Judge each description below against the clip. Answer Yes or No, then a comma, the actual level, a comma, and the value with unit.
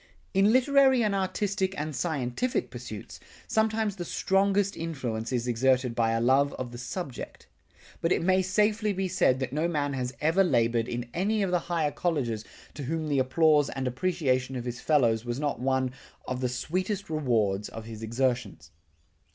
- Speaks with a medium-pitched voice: Yes, medium, 145 Hz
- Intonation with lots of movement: Yes, wide, 7.1 semitones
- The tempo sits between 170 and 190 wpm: Yes, average, 175 wpm